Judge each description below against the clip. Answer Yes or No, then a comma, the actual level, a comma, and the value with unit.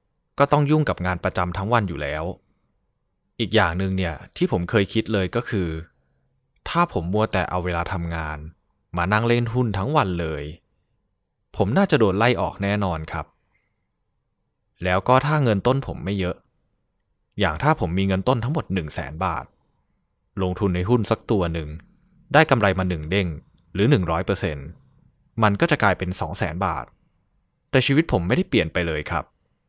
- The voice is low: Yes, very low, 95 Hz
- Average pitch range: Yes, average, 5.0 semitones